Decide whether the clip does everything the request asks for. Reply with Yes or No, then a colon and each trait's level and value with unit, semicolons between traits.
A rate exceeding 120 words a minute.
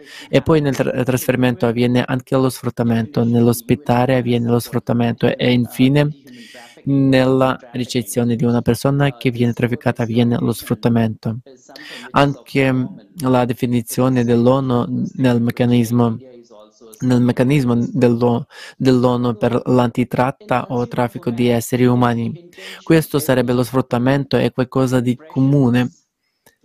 No: slow, 115 wpm